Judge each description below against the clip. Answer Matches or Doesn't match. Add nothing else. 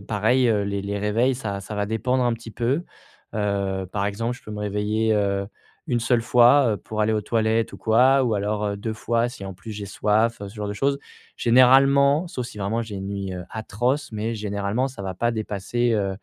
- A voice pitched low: Matches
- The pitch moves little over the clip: Doesn't match